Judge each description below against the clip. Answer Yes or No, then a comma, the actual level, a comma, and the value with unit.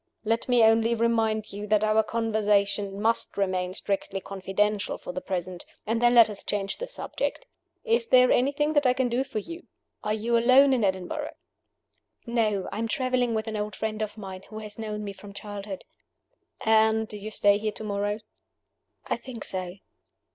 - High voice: Yes, high, 215 Hz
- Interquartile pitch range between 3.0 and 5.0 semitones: No, narrow, 2.4 semitones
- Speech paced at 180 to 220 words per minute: Yes, average, 185 wpm